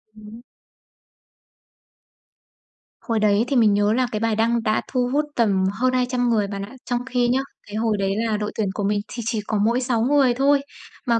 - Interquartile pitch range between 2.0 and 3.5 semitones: Yes, average, 2.9 semitones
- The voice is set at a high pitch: Yes, high, 230 Hz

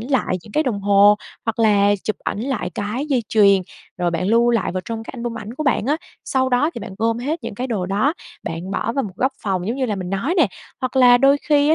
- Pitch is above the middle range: Yes, high, 230 Hz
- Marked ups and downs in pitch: No, average, 4.6 semitones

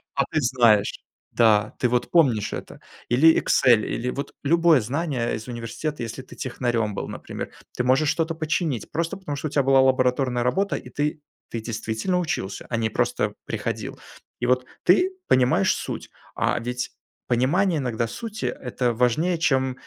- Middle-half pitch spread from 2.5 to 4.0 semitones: No, average, 4.8 semitones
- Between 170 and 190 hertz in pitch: No, low, 130 Hz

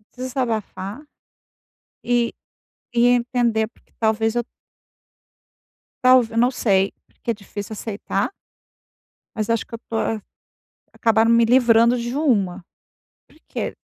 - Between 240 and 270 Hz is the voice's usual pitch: No, high, 230 Hz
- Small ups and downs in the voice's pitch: Yes, narrow, 1.9 semitones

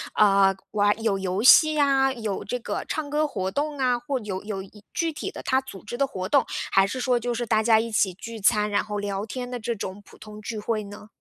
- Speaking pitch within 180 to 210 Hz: No, high, 220 Hz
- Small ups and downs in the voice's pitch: No, average, 4.2 semitones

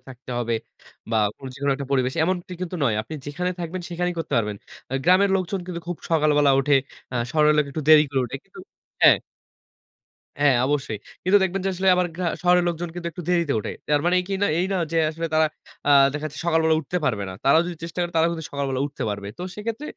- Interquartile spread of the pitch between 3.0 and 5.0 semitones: Yes, average, 4.0 semitones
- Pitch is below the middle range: No, medium, 160 Hz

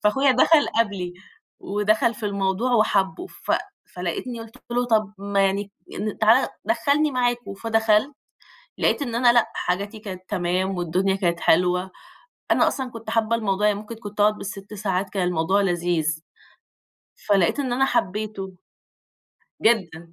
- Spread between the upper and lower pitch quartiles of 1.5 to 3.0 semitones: No, average, 3.4 semitones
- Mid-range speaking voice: No, high, 205 Hz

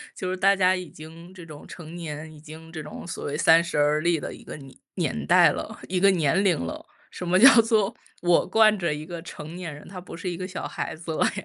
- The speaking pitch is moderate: Yes, medium, 170 Hz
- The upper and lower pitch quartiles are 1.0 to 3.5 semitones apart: Yes, average, 3.0 semitones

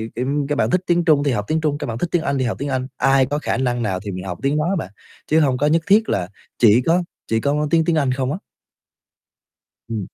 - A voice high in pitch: No, medium, 140 Hz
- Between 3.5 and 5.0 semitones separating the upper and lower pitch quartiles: Yes, average, 4.4 semitones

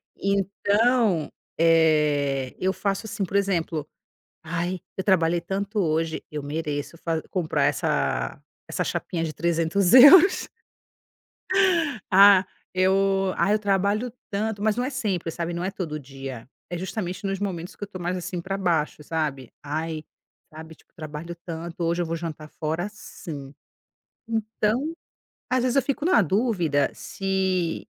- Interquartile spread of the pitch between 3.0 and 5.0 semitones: Yes, average, 3.8 semitones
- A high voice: No, medium, 180 Hz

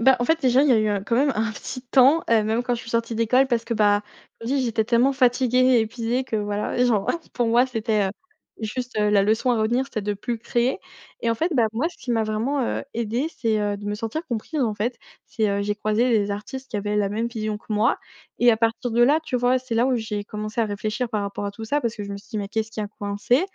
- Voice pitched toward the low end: No, high, 230 Hz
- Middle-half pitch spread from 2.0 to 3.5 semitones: Yes, average, 2.8 semitones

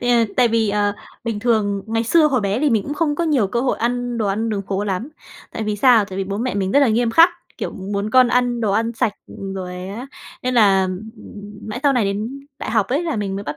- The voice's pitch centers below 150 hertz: No, high, 225 Hz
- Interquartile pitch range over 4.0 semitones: No, average, 3.7 semitones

